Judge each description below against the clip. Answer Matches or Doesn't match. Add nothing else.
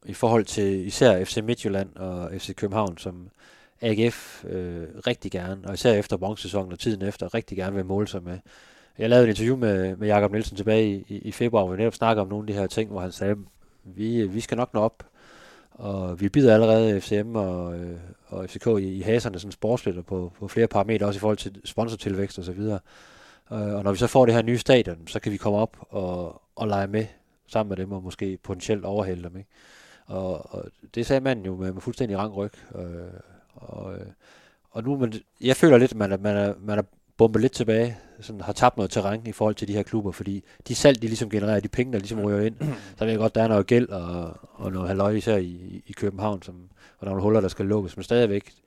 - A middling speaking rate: Doesn't match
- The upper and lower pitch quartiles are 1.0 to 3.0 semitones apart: Matches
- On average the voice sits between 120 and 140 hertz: Doesn't match